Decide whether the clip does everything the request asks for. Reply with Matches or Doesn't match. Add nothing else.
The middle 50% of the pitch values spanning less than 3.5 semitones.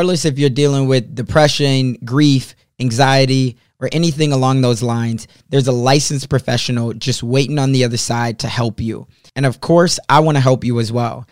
Matches